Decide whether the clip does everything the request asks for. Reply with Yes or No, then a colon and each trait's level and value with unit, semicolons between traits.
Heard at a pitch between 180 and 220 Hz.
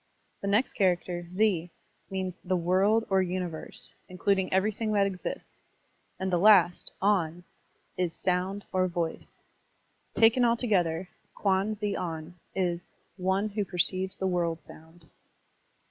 Yes: medium, 185 Hz